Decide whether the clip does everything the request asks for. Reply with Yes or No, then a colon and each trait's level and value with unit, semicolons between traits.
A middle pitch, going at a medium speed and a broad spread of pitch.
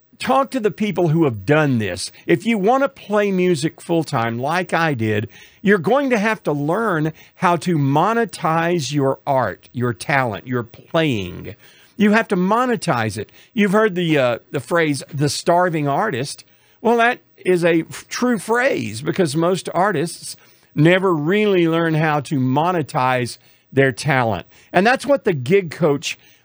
Yes: medium, 165 Hz; average, 170 wpm; wide, 6.1 semitones